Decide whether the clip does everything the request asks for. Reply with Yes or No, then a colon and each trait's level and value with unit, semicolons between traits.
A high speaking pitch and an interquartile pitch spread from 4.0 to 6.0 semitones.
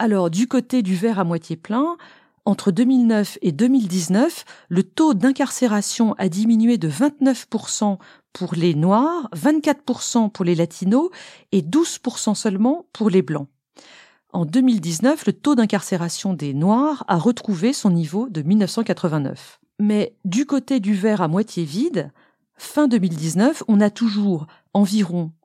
Yes: high, 210 Hz; average, 5.3 semitones